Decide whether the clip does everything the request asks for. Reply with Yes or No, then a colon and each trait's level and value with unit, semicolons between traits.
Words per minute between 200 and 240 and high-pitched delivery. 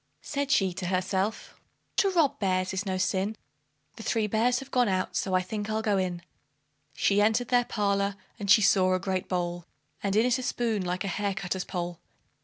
Yes: fast, 205 wpm; high, 200 Hz